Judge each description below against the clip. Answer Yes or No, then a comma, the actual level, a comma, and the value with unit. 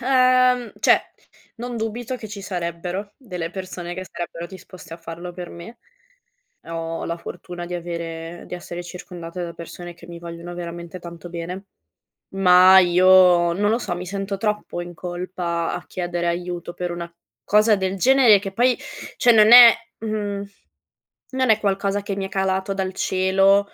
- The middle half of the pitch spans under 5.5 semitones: Yes, average, 2.8 semitones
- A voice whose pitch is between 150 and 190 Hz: Yes, medium, 185 Hz